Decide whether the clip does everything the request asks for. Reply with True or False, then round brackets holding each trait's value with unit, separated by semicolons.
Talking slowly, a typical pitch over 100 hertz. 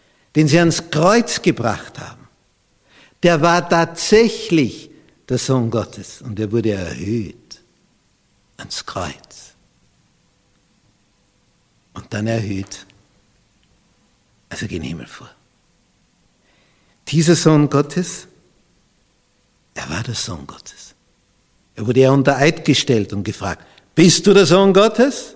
True (110 wpm; 140 Hz)